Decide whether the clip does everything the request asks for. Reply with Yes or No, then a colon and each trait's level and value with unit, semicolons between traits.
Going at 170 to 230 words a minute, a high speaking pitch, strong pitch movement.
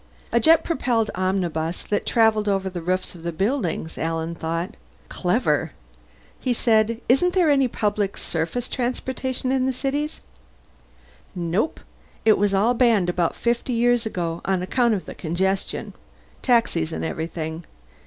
No: average, 145 wpm; high, 210 Hz; wide, 6.1 semitones